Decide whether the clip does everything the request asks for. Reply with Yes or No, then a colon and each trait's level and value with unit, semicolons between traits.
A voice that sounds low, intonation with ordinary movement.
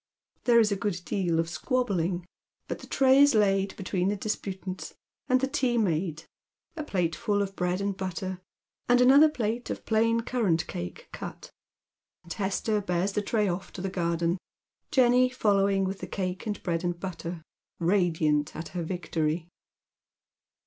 No: high, 195 Hz; average, 4.0 semitones